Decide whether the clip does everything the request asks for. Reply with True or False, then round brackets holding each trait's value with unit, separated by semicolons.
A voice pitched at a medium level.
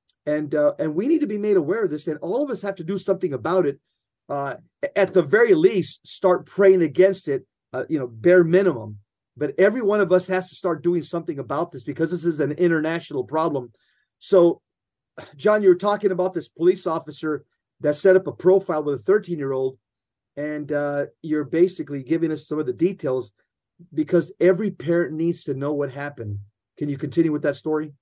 True (165 Hz)